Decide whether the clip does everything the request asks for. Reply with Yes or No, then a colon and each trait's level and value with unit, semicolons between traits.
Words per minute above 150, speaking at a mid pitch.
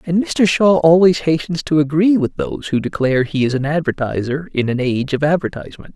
Yes: average, 200 wpm; medium, 155 Hz